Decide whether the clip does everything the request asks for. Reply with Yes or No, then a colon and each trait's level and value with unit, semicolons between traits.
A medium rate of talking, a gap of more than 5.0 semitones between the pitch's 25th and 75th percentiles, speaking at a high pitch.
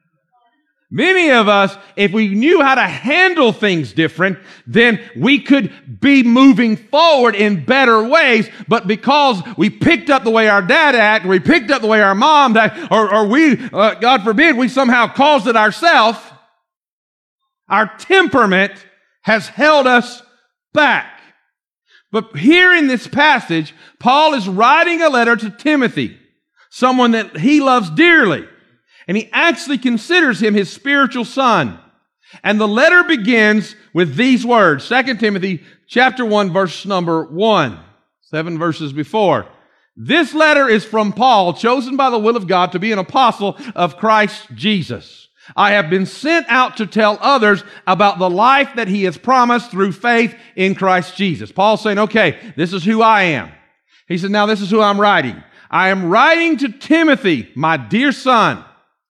Yes: average, 160 wpm; wide, 5.5 semitones; high, 220 Hz